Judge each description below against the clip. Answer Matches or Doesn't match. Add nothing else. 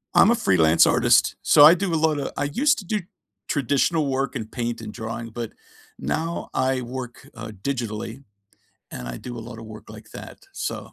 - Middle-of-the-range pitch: Doesn't match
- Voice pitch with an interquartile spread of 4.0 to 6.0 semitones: Matches